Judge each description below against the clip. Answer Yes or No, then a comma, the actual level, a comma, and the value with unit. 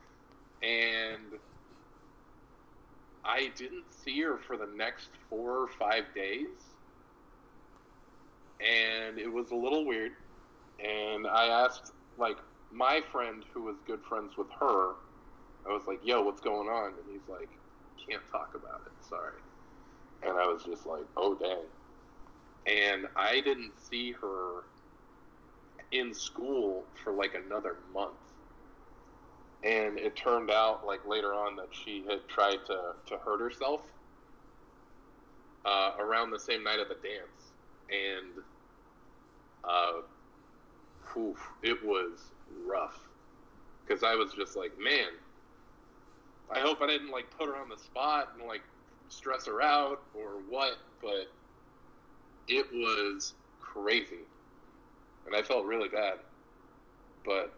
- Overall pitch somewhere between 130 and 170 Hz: Yes, medium, 140 Hz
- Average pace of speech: No, slow, 130 wpm